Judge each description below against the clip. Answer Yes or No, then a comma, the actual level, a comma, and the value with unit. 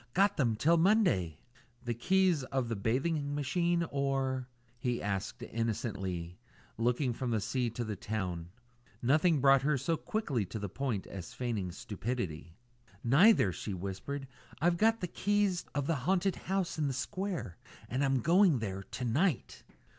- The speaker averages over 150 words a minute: Yes, average, 160 wpm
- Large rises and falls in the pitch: Yes, wide, 7.3 semitones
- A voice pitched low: Yes, low, 130 Hz